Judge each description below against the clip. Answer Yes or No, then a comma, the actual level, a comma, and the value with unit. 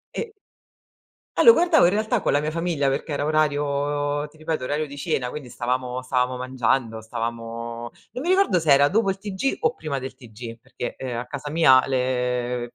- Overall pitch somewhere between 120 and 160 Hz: Yes, medium, 140 Hz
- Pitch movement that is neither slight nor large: Yes, average, 4.1 semitones